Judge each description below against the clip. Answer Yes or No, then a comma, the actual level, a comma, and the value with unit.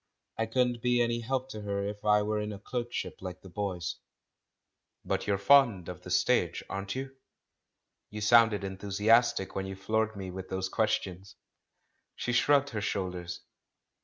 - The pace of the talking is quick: No, average, 160 wpm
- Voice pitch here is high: No, low, 105 Hz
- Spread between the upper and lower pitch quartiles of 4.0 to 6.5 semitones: No, average, 3.5 semitones